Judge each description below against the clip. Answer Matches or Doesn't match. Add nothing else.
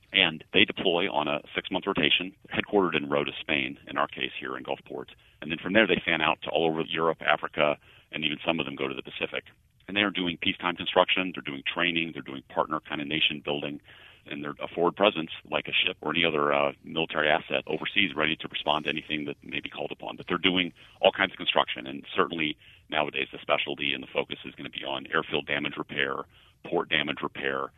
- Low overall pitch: Matches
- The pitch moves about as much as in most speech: Matches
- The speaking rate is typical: Doesn't match